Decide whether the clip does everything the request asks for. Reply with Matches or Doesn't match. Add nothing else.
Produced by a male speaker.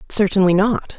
Doesn't match